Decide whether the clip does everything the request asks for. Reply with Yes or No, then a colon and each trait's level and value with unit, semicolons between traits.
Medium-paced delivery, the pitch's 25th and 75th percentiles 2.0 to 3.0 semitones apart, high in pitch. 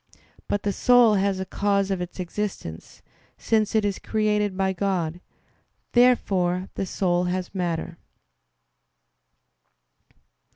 No: slow, 115 wpm; narrow, 2.5 semitones; high, 195 Hz